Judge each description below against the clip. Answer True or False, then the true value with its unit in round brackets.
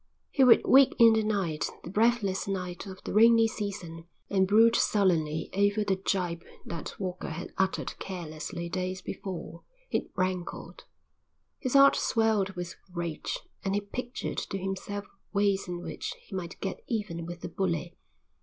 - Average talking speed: True (155 wpm)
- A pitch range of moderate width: True (3.2 semitones)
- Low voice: False (190 Hz)